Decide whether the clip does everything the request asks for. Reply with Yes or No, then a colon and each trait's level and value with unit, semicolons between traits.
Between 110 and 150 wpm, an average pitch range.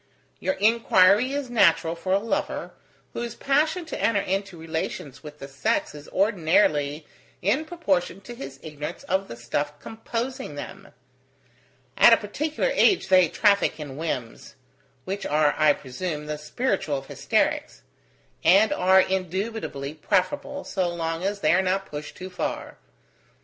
No: average, 145 wpm; wide, 6.6 semitones